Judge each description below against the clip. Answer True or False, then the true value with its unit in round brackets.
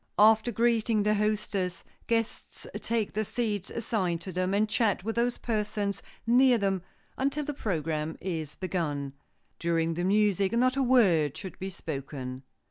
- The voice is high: True (205 Hz)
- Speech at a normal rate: True (150 wpm)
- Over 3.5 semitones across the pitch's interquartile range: True (4.8 semitones)